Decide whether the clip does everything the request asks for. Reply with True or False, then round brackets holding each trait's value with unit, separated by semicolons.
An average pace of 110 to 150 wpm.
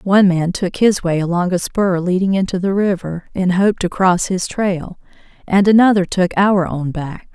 False (195 wpm)